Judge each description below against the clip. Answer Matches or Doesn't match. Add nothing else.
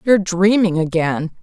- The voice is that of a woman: Matches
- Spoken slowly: Matches